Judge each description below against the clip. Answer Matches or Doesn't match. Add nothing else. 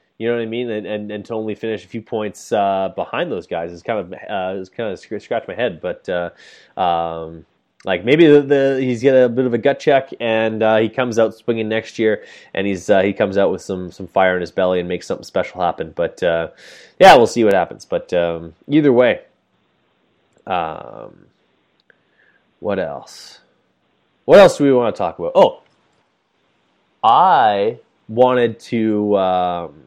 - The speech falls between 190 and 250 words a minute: Matches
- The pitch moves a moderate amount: Matches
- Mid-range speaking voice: Doesn't match